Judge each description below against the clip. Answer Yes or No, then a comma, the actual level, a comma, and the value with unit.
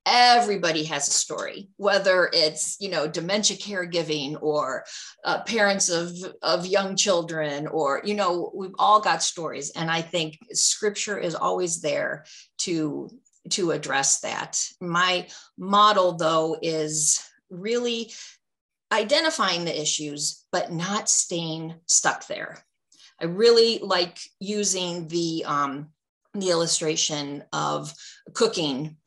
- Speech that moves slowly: Yes, slow, 120 wpm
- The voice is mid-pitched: Yes, medium, 175 Hz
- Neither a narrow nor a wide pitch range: Yes, average, 4.5 semitones